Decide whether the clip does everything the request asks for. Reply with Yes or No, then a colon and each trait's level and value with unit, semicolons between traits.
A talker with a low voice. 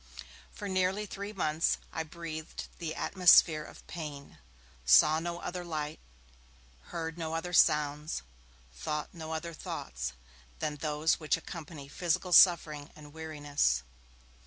No: medium, 160 Hz